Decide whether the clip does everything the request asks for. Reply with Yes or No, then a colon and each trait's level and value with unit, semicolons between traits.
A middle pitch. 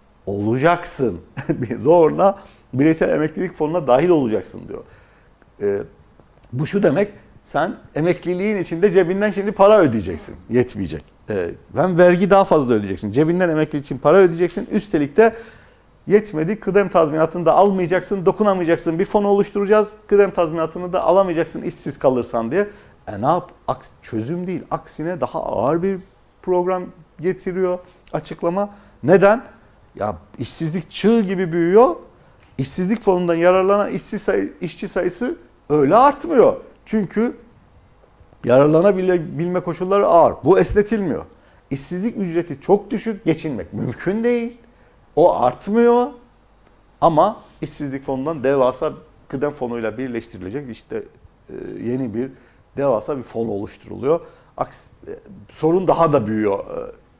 Yes: medium, 180 Hz